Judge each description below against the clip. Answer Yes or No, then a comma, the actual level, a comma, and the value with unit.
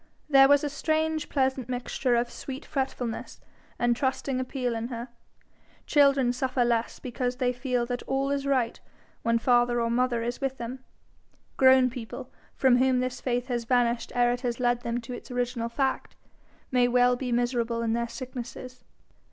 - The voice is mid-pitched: No, very high, 250 Hz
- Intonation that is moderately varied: No, narrow, 1.7 semitones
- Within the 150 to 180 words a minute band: Yes, average, 170 wpm